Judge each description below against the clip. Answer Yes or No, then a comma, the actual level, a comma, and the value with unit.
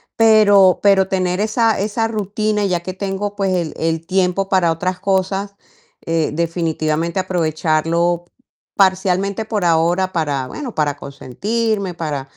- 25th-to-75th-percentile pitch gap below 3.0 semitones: No, average, 3.4 semitones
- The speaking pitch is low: No, medium, 185 Hz